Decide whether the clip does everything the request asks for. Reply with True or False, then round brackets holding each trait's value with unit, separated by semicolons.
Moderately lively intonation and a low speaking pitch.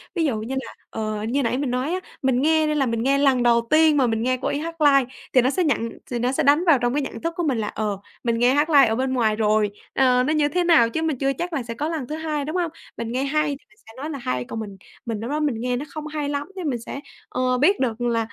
False (4.4 semitones; 265 Hz)